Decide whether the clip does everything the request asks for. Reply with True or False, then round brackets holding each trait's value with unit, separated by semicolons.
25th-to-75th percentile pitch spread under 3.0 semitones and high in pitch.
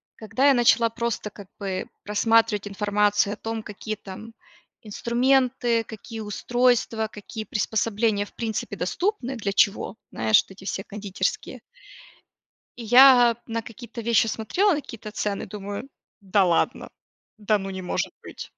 True (2.5 semitones; 220 Hz)